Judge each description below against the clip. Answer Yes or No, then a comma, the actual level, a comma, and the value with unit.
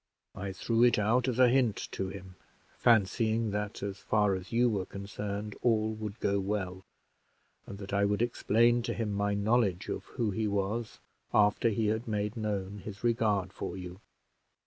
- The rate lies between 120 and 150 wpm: No, average, 175 wpm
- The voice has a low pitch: Yes, low, 105 Hz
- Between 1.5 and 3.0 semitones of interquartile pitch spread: Yes, narrow, 2.4 semitones